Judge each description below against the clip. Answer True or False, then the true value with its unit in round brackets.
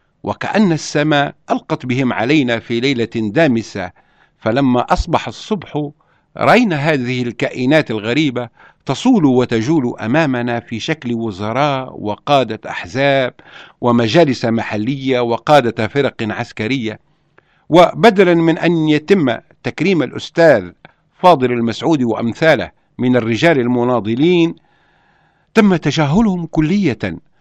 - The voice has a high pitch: False (135 Hz)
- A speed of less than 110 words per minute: True (95 wpm)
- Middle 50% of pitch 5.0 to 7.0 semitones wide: True (5.4 semitones)